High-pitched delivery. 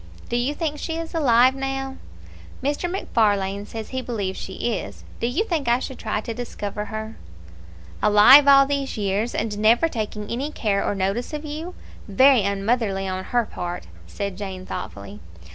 Yes: high, 230 Hz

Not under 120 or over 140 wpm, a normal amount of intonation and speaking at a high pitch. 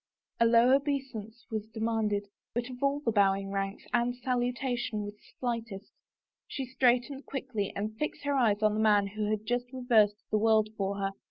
No: average, 185 wpm; average, 3.1 semitones; high, 225 Hz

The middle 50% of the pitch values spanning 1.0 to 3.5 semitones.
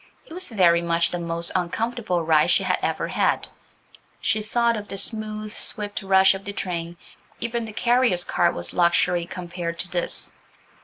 No: average, 4.1 semitones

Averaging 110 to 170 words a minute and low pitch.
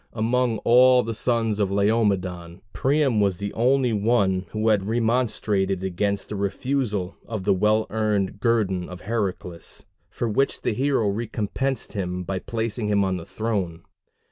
Yes: average, 150 wpm; low, 105 Hz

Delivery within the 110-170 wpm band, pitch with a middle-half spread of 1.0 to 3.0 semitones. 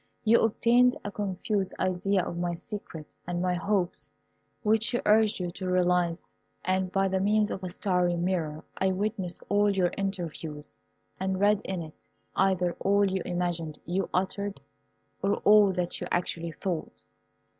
Yes: average, 155 wpm; narrow, 2.5 semitones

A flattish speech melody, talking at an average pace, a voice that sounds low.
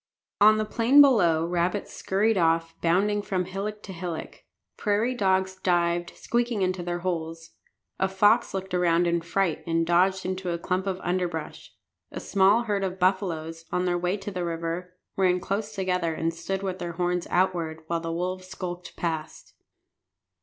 No: narrow, 2.2 semitones; average, 165 wpm; medium, 180 Hz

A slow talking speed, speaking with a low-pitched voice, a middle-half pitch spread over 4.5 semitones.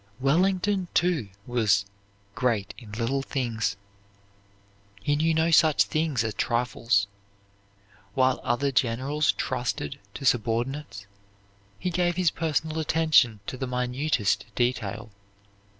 Yes: slow, 110 wpm; low, 130 Hz; average, 5.2 semitones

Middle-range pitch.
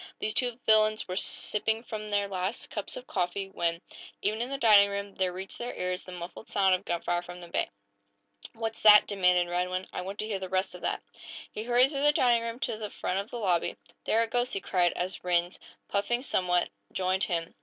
No: high, 200 Hz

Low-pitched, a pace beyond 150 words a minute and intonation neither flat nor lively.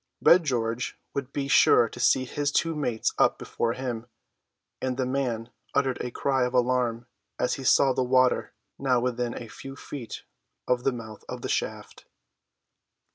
No: low, 125 Hz; average, 170 wpm; narrow, 2.2 semitones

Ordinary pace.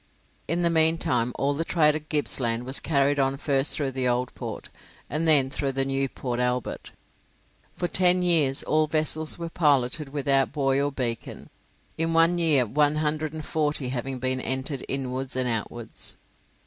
Yes: average, 170 wpm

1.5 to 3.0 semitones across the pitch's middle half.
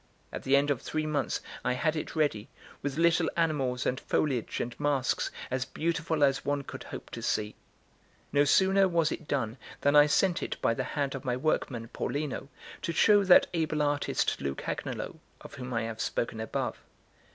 No: average, 3.7 semitones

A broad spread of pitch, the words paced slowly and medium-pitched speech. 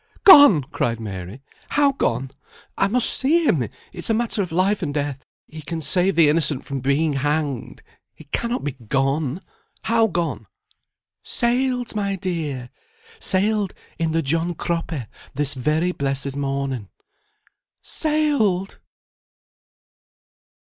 Yes: wide, 6.6 semitones; slow, 125 wpm; medium, 160 Hz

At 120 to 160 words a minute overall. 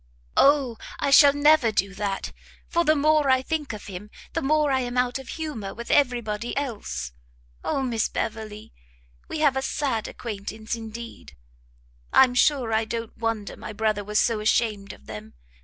No: average, 175 wpm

